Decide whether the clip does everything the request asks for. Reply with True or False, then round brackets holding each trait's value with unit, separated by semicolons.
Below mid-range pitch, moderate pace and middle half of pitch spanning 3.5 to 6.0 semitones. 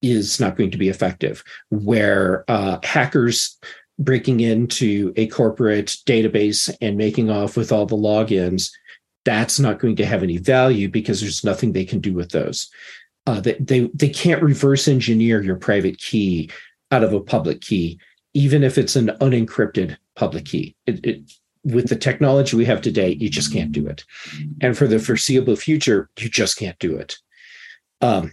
True (115 Hz; 175 wpm; 4.5 semitones)